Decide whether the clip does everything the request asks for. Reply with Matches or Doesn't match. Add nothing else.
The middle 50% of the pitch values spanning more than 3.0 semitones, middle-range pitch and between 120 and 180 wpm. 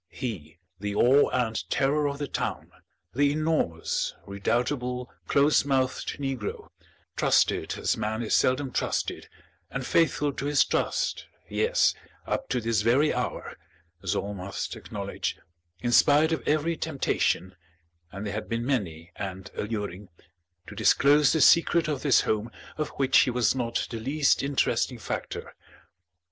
Doesn't match